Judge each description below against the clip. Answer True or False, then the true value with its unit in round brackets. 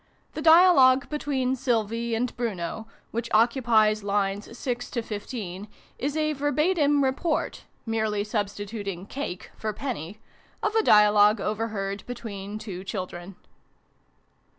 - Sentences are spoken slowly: True (120 wpm)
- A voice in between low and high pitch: False (225 Hz)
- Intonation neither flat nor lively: True (4.3 semitones)